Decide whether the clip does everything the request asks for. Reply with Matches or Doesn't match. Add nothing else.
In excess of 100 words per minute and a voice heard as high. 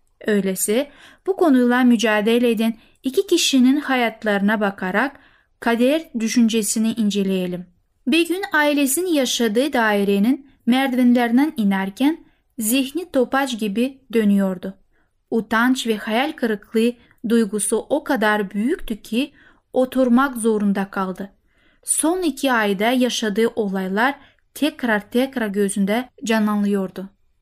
Doesn't match